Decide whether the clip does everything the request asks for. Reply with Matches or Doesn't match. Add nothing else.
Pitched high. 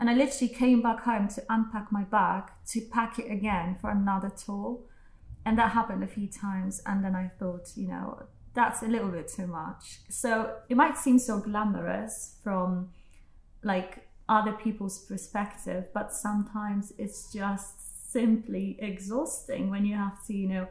Matches